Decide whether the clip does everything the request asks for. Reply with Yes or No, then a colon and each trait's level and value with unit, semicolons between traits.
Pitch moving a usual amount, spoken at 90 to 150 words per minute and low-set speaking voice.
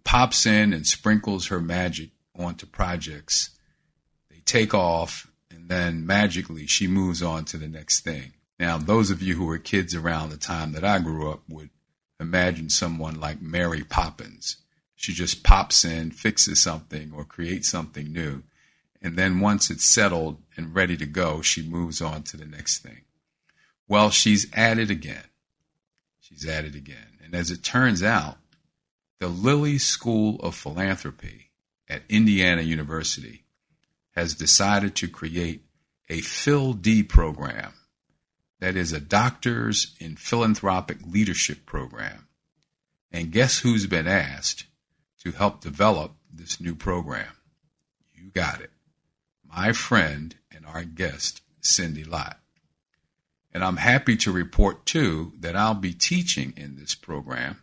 Yes: average, 3.8 semitones; average, 145 wpm; very low, 85 Hz